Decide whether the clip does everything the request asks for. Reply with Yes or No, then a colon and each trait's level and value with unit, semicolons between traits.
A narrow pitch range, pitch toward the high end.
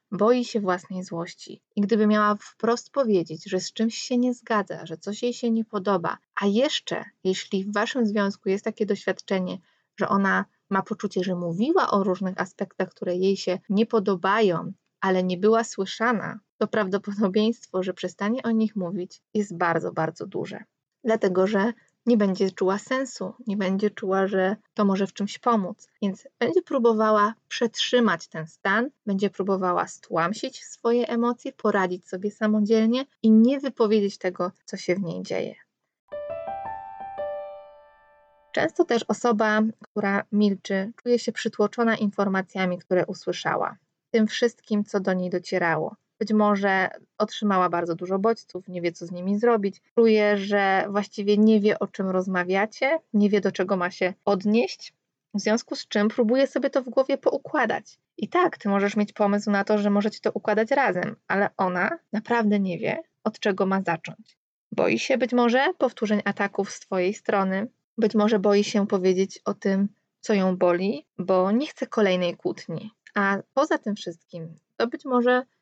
No: average, 3.1 semitones; high, 205 Hz